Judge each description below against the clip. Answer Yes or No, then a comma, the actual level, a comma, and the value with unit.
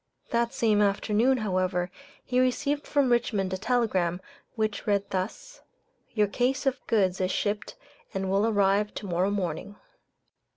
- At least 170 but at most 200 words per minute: No, average, 140 wpm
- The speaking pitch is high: Yes, high, 205 Hz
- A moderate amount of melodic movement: Yes, average, 3.8 semitones